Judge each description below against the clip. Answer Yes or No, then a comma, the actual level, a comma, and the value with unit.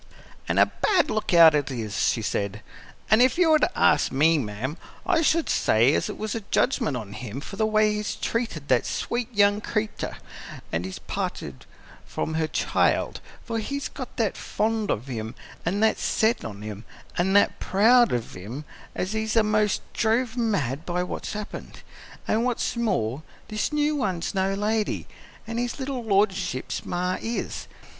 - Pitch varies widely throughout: Yes, wide, 8.6 semitones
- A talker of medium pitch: No, high, 205 Hz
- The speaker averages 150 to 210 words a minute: Yes, average, 170 wpm